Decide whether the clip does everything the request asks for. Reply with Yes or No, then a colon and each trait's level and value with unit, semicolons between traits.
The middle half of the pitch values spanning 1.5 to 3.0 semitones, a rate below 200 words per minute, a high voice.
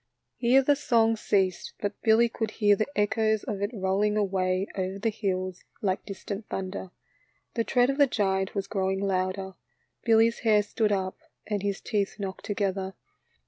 Yes: narrow, 2.5 semitones; average, 165 wpm; high, 205 Hz